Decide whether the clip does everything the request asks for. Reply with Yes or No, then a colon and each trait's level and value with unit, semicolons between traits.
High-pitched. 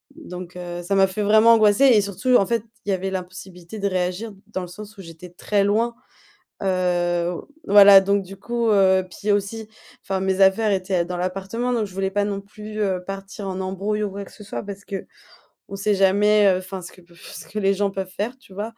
Yes: high, 195 Hz